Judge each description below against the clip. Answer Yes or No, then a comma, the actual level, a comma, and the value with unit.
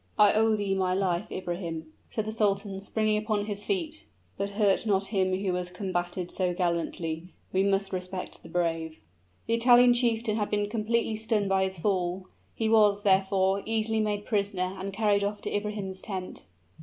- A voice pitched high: Yes, high, 200 Hz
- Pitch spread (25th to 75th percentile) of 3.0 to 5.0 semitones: No, narrow, 2.4 semitones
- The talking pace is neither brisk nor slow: Yes, average, 175 wpm